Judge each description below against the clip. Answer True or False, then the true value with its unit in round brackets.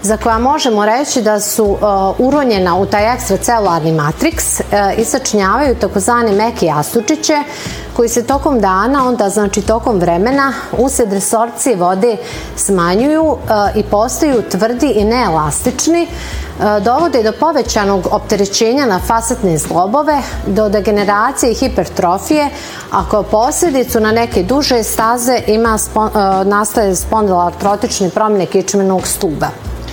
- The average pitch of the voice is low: False (220 Hz)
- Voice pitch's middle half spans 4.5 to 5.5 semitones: False (3.8 semitones)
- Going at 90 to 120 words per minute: True (110 wpm)